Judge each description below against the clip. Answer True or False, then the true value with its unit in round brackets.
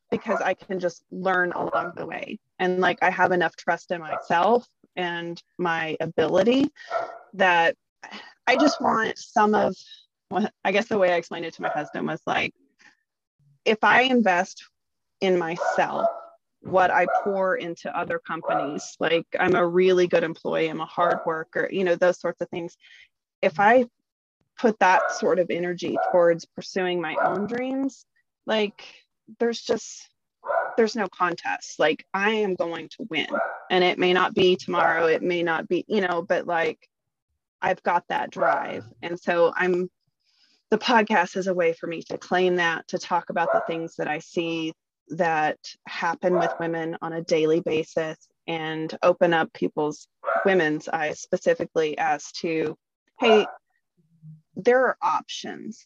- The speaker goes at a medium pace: True (160 wpm)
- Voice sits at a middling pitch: True (180 Hz)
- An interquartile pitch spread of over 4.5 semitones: False (3.9 semitones)